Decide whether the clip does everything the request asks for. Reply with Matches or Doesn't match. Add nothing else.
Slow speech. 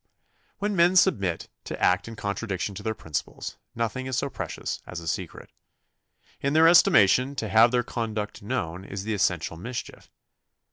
Doesn't match